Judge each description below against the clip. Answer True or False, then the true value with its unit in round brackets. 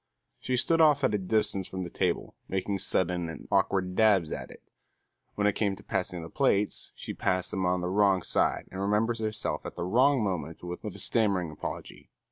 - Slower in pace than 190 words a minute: False (200 wpm)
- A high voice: False (95 Hz)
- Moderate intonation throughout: True (3.1 semitones)